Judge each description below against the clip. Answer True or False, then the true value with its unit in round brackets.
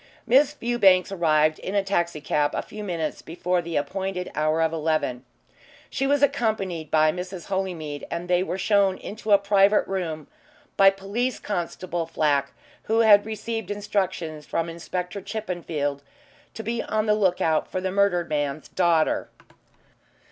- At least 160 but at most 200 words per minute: False (150 wpm)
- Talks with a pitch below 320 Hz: True (185 Hz)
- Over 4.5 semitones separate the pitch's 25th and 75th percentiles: False (4.2 semitones)